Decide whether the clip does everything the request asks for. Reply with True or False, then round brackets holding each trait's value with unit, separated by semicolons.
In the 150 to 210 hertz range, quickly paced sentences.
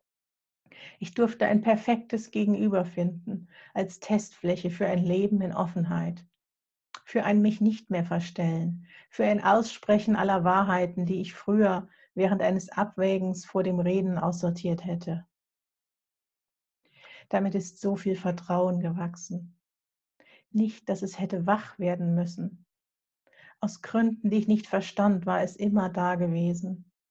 False (190 Hz; 130 wpm)